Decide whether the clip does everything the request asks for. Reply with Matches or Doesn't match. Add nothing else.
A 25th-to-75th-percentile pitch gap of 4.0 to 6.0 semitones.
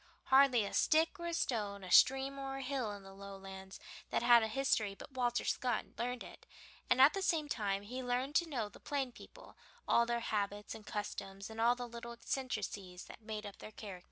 Matches